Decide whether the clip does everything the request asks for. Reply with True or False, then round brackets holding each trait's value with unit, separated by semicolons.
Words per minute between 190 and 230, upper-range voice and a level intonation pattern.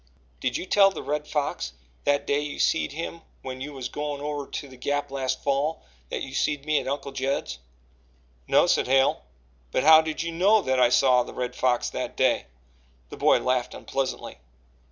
False (195 wpm; 140 Hz; 2.3 semitones)